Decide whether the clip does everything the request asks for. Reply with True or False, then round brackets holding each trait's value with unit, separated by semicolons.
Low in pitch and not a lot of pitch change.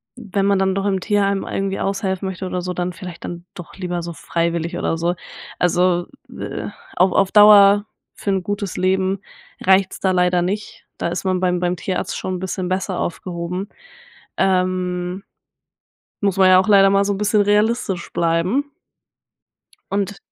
False (185 Hz; 1.8 semitones)